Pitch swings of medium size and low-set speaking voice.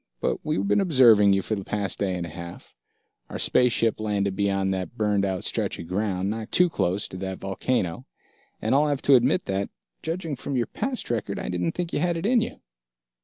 No: wide, 5.7 semitones; low, 105 Hz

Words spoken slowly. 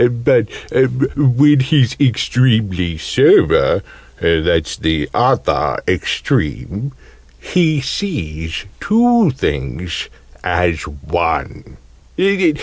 Yes: slow, 70 wpm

